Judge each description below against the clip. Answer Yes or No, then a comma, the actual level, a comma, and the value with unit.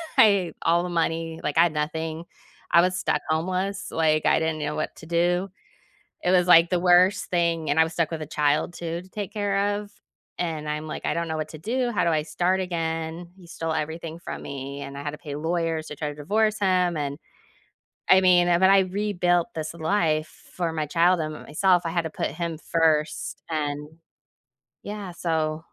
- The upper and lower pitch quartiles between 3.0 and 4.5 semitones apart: No, narrow, 2.6 semitones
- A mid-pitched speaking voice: Yes, medium, 165 Hz